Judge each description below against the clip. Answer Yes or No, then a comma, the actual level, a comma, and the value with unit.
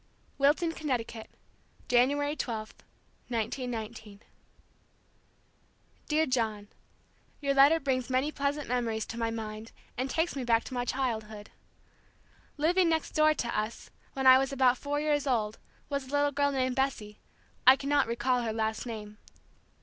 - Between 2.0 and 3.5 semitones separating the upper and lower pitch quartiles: No, average, 4.1 semitones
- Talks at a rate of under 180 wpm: Yes, average, 140 wpm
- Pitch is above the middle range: Yes, very high, 255 Hz